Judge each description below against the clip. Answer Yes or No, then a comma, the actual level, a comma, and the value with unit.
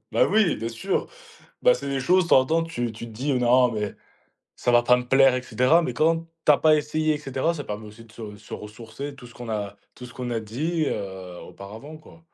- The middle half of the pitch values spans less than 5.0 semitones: No, wide, 5.5 semitones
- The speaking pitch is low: Yes, low, 125 Hz